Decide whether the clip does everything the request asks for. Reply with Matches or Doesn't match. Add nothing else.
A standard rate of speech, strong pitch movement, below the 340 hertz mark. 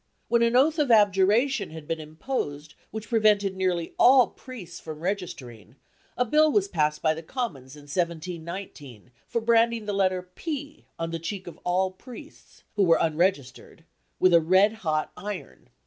Matches